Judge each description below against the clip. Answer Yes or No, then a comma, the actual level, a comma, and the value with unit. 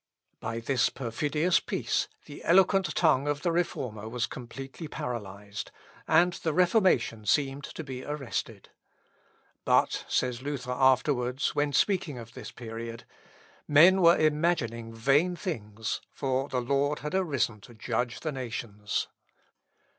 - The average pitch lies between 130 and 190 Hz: Yes, low, 135 Hz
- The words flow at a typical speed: No, slow, 130 wpm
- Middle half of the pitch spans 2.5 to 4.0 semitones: No, average, 4.8 semitones